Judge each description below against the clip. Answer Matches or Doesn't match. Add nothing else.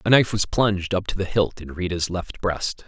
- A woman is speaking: Doesn't match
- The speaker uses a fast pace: Matches